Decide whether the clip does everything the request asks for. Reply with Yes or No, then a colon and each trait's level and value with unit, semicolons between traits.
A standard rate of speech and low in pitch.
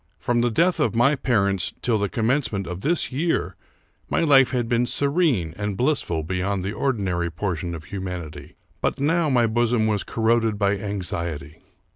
Yes: average, 165 wpm; low, 110 Hz